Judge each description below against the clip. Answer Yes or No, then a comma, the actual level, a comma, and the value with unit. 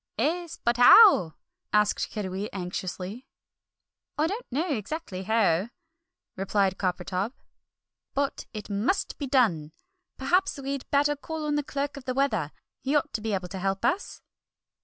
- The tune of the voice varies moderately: No, wide, 7.0 semitones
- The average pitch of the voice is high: Yes, high, 235 Hz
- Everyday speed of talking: Yes, average, 145 wpm